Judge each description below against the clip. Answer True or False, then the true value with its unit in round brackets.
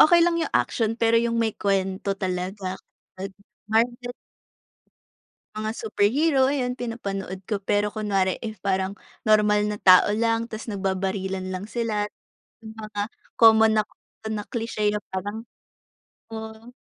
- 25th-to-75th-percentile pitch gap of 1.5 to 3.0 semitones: True (2.7 semitones)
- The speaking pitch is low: False (215 Hz)